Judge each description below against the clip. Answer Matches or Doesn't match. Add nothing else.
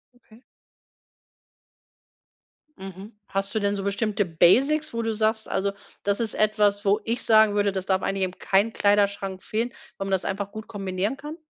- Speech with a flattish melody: Matches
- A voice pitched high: Matches